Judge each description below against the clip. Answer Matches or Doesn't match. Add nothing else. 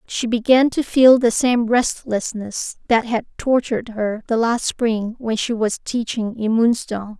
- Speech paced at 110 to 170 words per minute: Matches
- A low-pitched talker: Doesn't match